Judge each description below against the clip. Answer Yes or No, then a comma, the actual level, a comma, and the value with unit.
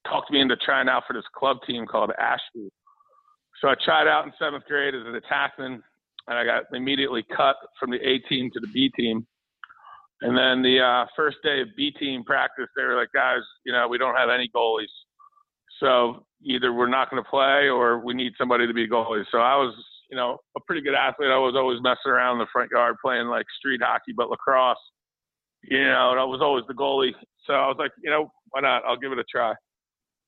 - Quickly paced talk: Yes, fast, 230 wpm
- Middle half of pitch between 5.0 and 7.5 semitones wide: Yes, wide, 5.4 semitones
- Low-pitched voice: Yes, low, 130 Hz